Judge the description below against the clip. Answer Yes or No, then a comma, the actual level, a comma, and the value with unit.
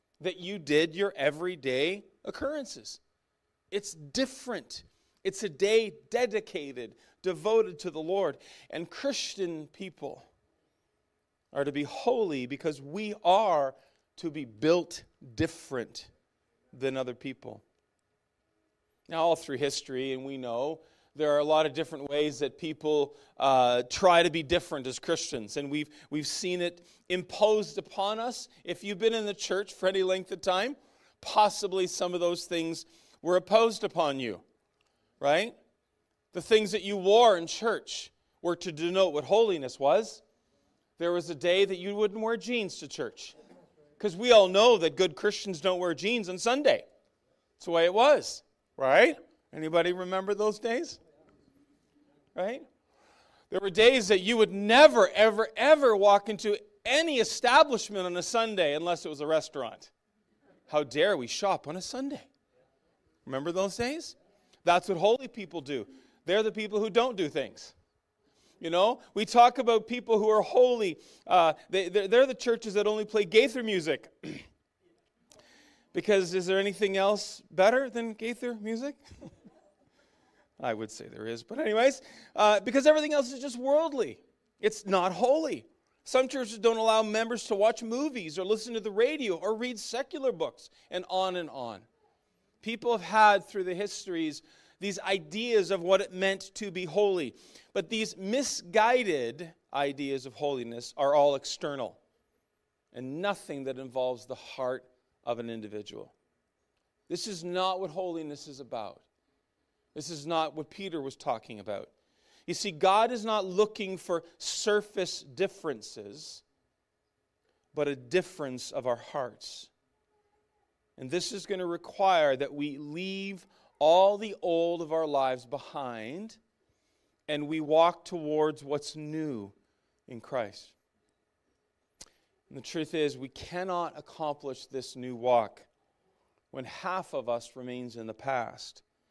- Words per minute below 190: Yes, average, 150 wpm